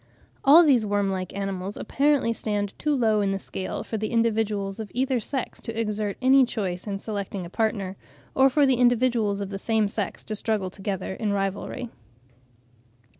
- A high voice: Yes, high, 215 Hz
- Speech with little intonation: No, average, 3.5 semitones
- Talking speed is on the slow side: No, average, 175 wpm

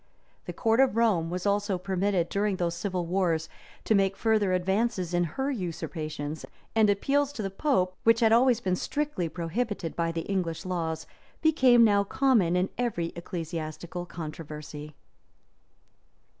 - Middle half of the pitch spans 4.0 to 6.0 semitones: Yes, average, 4.8 semitones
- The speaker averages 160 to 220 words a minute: No, average, 145 wpm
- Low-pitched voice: No, medium, 185 Hz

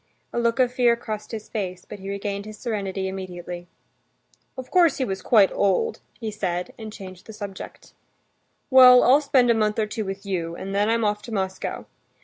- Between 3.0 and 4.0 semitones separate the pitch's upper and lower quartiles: Yes, average, 3.4 semitones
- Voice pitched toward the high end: Yes, high, 210 Hz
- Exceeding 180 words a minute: Yes, average, 195 wpm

